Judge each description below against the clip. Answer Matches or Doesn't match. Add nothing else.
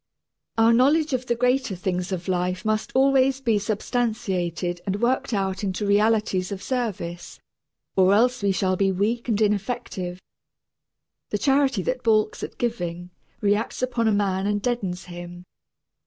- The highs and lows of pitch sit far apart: Doesn't match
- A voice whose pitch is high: Matches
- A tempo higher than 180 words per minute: Doesn't match